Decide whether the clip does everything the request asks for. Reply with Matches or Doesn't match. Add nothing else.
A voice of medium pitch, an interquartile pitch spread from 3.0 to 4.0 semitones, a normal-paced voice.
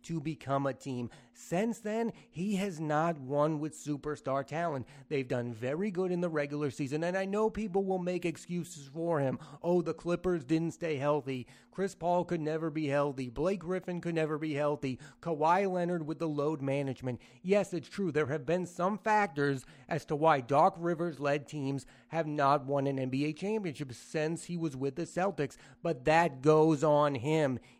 Matches